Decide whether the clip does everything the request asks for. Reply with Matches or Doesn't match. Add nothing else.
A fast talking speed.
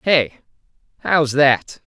Doesn't match